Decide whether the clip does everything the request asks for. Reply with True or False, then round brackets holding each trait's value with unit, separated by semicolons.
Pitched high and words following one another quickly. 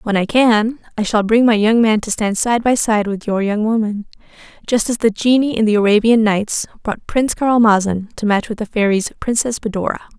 True (220 Hz; 210 wpm)